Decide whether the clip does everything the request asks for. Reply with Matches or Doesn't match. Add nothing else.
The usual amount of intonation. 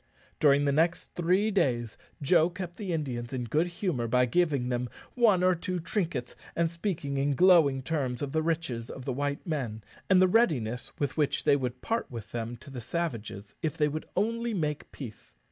Doesn't match